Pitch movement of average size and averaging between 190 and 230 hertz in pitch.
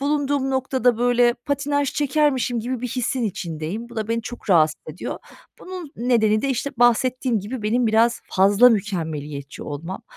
No: average, 4.3 semitones; high, 240 Hz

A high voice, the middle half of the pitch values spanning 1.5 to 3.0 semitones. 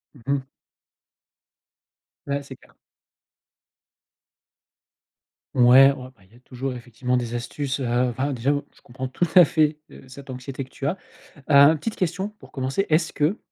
No: low, 135 Hz; narrow, 2.6 semitones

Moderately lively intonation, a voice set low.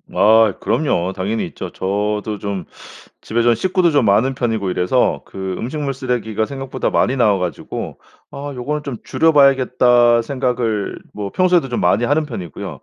Yes: average, 4.6 semitones; low, 120 Hz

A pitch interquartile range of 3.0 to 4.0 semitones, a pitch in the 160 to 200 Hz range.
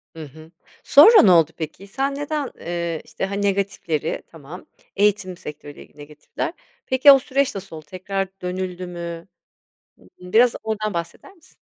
No: average, 4.7 semitones; medium, 185 Hz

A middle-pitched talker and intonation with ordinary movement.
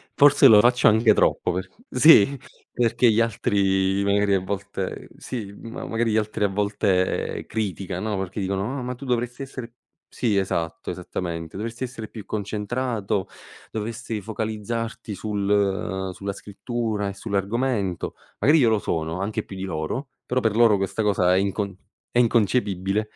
No: low, 105 Hz; average, 3.1 semitones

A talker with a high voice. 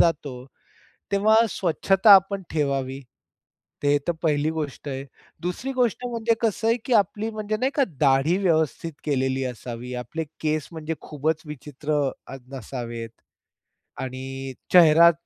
No: medium, 155 Hz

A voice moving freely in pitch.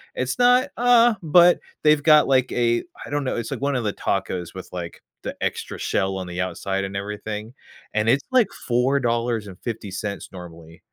Yes: wide, 6.7 semitones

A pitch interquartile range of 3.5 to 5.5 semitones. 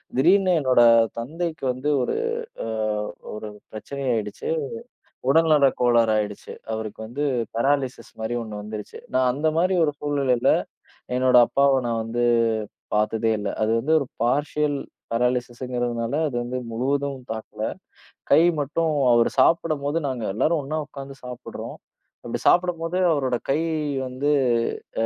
Yes: average, 3.9 semitones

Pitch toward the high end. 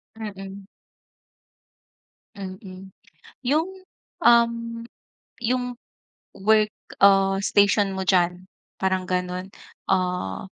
Yes: high, 195 Hz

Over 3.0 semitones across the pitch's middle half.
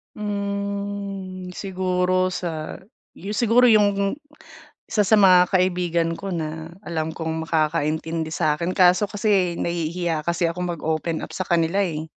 Yes: average, 3.4 semitones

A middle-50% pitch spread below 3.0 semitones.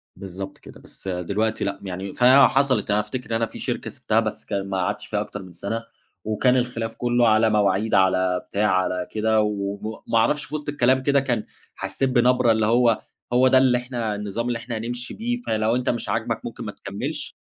No: average, 3.7 semitones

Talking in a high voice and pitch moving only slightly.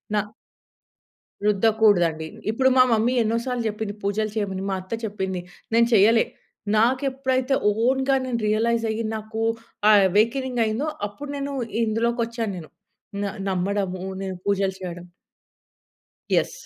No: high, 220 Hz; average, 3.0 semitones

